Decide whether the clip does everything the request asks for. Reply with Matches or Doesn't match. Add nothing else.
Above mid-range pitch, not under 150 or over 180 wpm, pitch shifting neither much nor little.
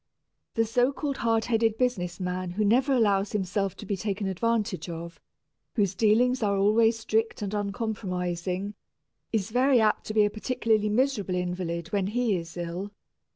Matches